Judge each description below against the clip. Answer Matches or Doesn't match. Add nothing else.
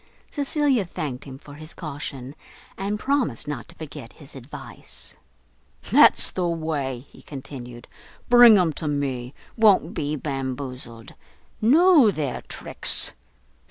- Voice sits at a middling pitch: Matches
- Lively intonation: Matches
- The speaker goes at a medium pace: Doesn't match